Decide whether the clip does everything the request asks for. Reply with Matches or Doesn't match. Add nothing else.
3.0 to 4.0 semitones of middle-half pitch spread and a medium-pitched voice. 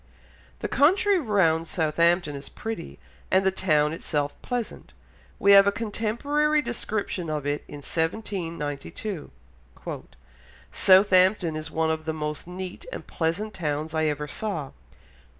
Doesn't match